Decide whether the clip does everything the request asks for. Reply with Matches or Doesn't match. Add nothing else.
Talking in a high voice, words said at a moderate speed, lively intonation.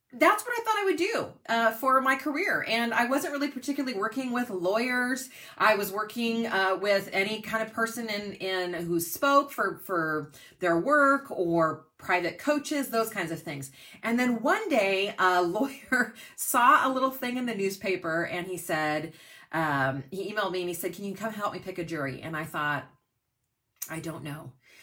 Matches